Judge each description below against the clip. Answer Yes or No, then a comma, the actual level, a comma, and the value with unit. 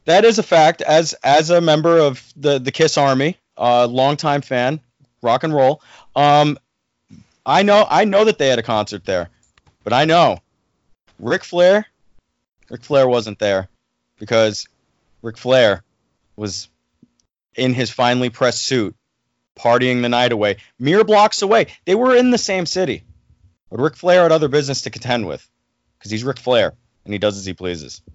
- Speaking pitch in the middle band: No, low, 125 Hz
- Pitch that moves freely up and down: Yes, wide, 6.2 semitones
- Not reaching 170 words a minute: No, average, 175 wpm